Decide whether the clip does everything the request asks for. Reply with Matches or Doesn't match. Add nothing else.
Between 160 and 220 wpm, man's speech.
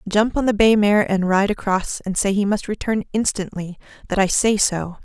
Doesn't match